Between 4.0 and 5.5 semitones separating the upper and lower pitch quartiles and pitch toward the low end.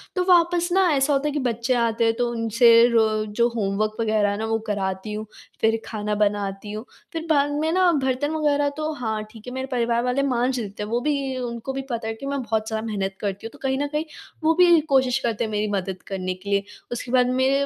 No: average, 4.3 semitones; high, 235 Hz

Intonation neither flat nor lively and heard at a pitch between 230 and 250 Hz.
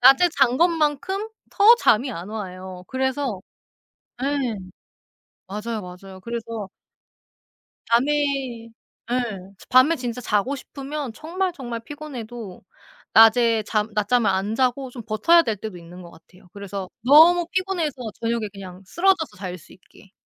No: wide, 5.9 semitones; high, 235 Hz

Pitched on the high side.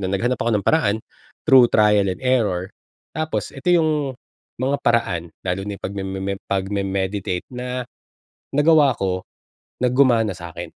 No: low, 105 Hz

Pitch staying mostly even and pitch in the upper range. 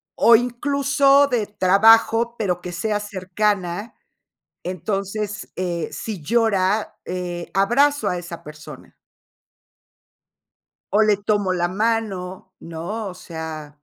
No: average, 3.9 semitones; high, 200 Hz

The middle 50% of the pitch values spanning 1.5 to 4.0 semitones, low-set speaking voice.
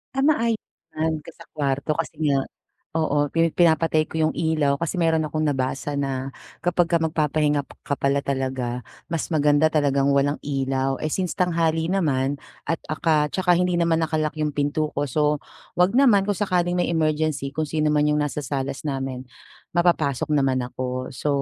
No: average, 2.9 semitones; medium, 150 Hz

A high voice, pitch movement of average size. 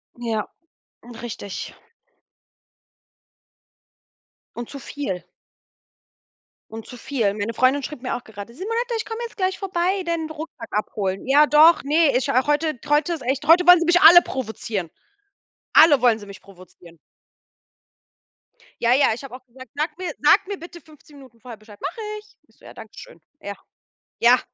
No: very high, 280 Hz; wide, 6.5 semitones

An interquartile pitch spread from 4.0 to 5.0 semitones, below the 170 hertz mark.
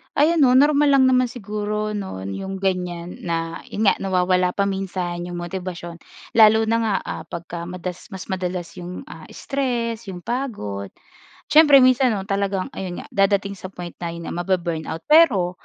No: average, 4.3 semitones; high, 190 Hz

